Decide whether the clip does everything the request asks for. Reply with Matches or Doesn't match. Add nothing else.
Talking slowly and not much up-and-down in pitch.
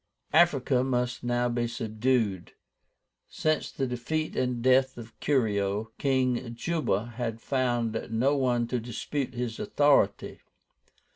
Matches